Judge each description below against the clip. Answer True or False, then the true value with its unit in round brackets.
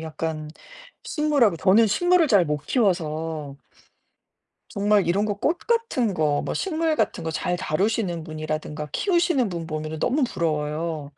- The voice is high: False (175 Hz)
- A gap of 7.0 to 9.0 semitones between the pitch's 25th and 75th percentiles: True (7.8 semitones)